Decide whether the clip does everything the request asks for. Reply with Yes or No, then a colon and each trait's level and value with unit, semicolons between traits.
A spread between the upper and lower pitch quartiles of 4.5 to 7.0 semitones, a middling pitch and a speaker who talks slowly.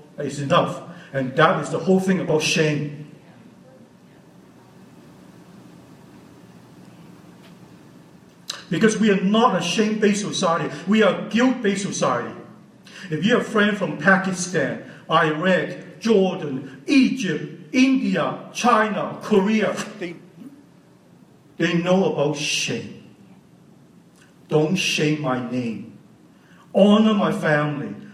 Yes: average, 4.8 semitones; medium, 180 Hz; slow, 100 wpm